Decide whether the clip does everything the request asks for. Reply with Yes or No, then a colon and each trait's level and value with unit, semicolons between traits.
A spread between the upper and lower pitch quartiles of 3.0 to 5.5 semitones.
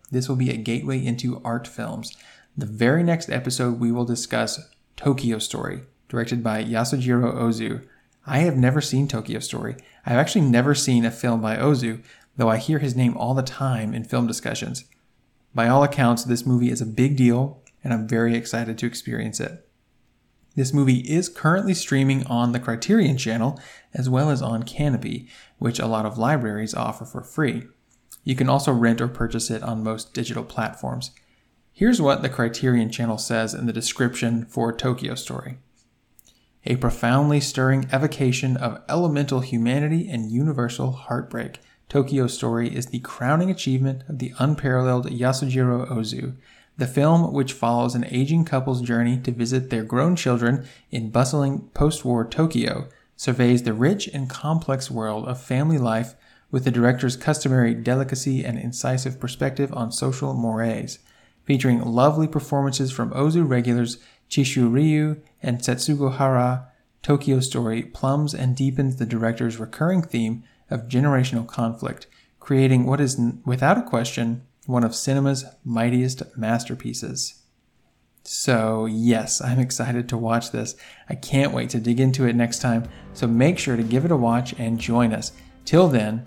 No: narrow, 2.5 semitones